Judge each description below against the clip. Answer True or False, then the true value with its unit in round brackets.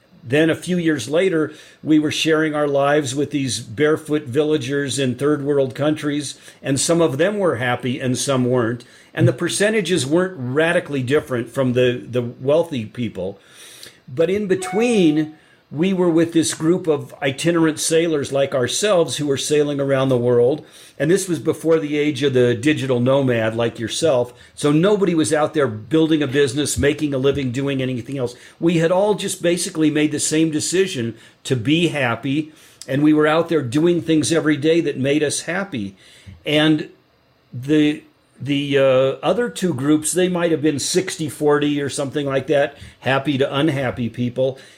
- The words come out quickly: False (170 wpm)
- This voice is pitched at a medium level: True (150 Hz)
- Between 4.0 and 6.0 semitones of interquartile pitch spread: False (3.1 semitones)